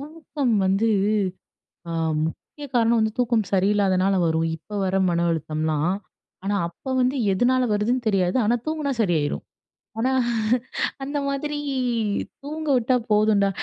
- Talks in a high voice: Yes, high, 215 Hz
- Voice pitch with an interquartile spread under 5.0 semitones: No, wide, 5.5 semitones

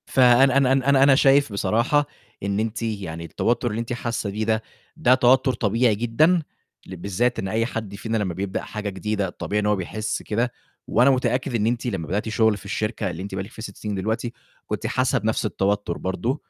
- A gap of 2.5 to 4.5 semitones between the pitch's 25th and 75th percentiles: Yes, average, 3.5 semitones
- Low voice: Yes, low, 110 Hz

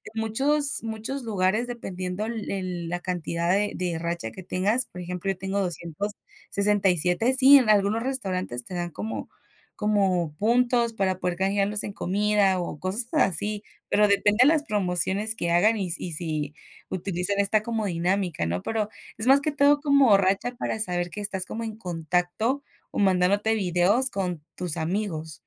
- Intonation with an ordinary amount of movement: Yes, average, 3.8 semitones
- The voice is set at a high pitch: Yes, high, 195 Hz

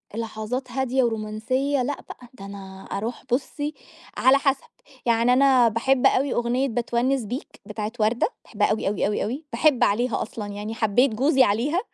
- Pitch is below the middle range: No, high, 240 Hz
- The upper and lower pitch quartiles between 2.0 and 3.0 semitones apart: No, average, 3.6 semitones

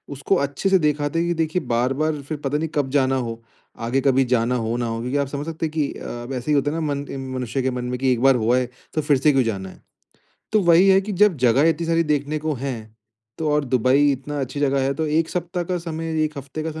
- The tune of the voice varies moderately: Yes, average, 3.7 semitones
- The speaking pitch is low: No, medium, 145 Hz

